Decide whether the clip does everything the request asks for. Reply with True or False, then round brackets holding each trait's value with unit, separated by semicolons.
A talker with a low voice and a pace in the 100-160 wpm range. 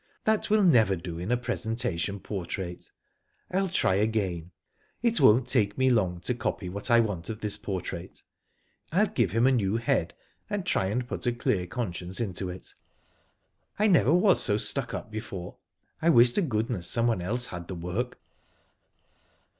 False (110 Hz; 170 wpm)